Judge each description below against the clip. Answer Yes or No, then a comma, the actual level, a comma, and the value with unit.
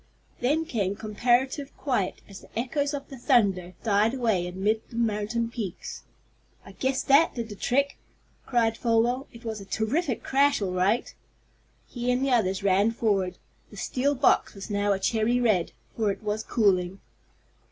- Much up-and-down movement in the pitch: No, average, 3.9 semitones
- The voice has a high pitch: Yes, high, 225 Hz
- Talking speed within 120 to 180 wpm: Yes, average, 165 wpm